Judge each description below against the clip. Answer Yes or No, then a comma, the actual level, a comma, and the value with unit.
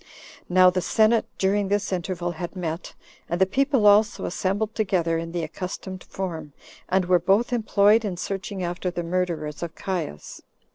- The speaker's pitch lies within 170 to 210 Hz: Yes, medium, 185 Hz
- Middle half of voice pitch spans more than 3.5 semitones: No, average, 2.8 semitones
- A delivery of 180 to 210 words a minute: No, average, 160 wpm